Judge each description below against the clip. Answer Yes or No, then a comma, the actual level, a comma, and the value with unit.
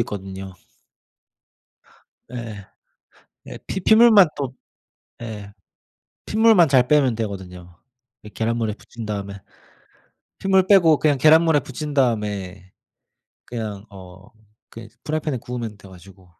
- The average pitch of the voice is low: Yes, low, 115 Hz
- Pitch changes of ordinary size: No, wide, 7.2 semitones